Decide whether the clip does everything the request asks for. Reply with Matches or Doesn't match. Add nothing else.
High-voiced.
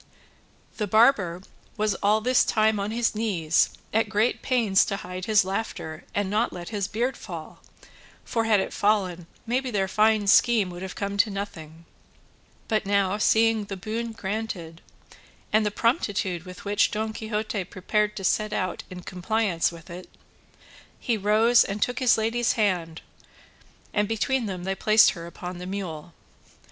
Matches